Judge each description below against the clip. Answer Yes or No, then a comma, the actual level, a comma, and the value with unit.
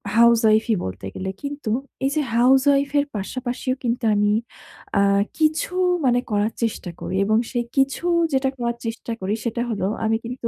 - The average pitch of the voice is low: No, high, 235 Hz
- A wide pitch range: No, average, 3.6 semitones